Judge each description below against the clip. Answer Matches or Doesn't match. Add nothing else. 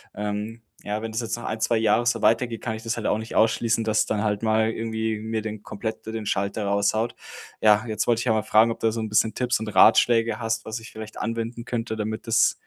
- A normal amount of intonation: Doesn't match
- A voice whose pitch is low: Matches